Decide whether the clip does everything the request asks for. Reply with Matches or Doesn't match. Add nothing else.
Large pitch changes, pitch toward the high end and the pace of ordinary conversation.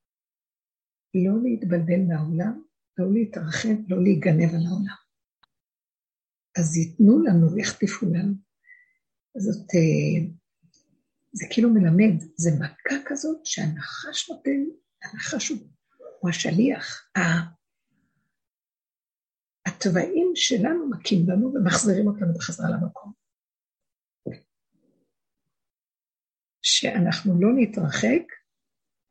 Doesn't match